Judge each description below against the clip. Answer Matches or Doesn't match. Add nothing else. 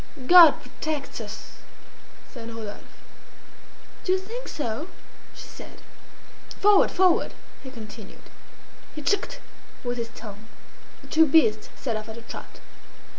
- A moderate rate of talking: Doesn't match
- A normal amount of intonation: Doesn't match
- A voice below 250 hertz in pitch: Doesn't match